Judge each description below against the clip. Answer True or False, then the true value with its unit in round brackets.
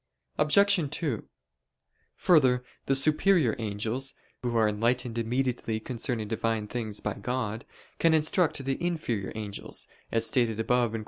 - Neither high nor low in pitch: False (120 Hz)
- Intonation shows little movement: False (3.8 semitones)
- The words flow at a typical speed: False (130 wpm)